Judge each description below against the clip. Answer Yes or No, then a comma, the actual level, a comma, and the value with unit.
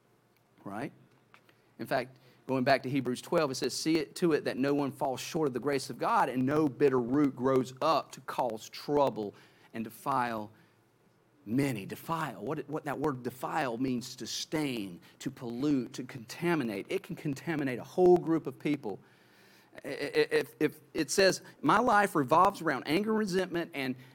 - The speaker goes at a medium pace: Yes, average, 170 wpm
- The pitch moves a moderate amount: Yes, average, 3.9 semitones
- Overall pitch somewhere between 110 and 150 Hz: Yes, medium, 140 Hz